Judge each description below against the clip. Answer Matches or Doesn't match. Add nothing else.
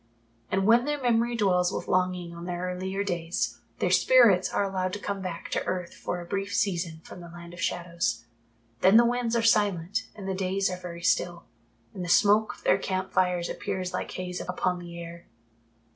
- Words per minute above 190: Matches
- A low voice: Doesn't match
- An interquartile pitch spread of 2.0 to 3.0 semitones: Matches